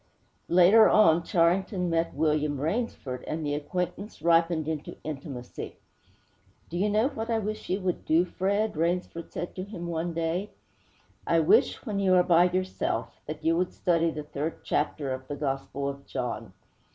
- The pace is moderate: Yes, average, 165 wpm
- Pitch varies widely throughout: No, average, 3.4 semitones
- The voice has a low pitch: No, medium, 170 Hz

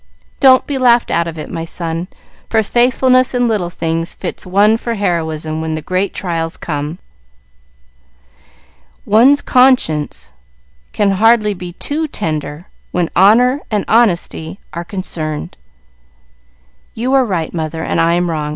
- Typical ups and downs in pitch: No, wide, 6.2 semitones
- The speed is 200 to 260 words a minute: No, average, 140 wpm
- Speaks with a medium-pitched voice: Yes, medium, 180 Hz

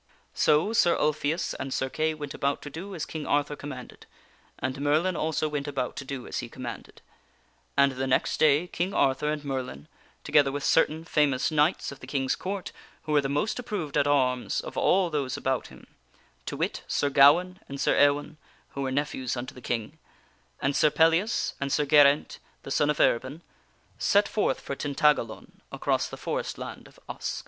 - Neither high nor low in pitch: Yes, medium, 145 Hz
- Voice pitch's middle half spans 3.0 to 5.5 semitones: No, narrow, 2.5 semitones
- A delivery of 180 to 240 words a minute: Yes, average, 190 wpm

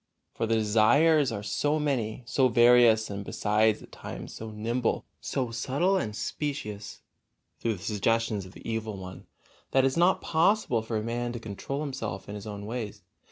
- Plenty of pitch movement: No, average, 3.7 semitones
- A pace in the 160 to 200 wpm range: Yes, average, 180 wpm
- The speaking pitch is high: No, low, 115 Hz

